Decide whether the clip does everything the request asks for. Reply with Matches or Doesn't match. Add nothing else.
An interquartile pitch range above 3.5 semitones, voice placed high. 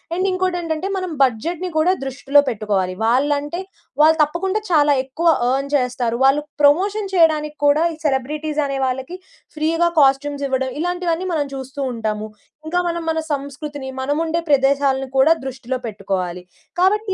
Matches